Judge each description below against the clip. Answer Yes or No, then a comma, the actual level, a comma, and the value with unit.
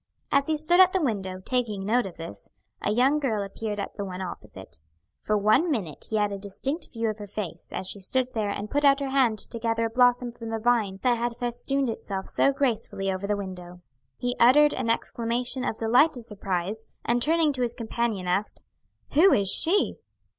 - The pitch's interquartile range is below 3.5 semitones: No, average, 4.2 semitones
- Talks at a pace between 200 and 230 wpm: Yes, fast, 205 wpm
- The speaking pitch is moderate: No, high, 230 Hz